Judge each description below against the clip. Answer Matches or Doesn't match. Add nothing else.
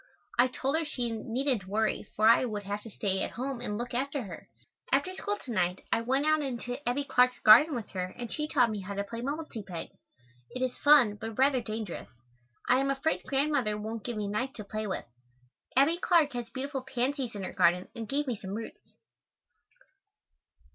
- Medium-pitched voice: Doesn't match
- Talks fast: Matches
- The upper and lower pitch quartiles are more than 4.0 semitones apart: Matches